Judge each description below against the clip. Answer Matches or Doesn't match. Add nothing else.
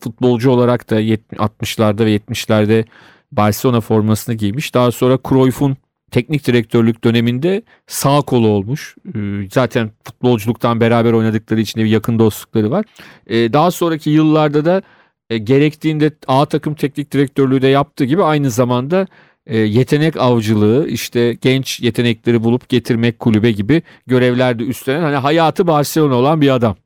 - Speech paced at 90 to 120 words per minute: Doesn't match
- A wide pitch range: Doesn't match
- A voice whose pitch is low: Matches